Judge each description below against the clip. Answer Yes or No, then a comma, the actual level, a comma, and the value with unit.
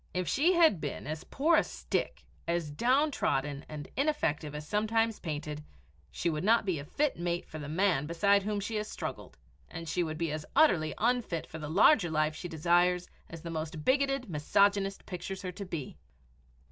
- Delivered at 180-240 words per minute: Yes, average, 185 wpm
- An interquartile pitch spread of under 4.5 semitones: No, wide, 5.4 semitones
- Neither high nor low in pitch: Yes, medium, 175 Hz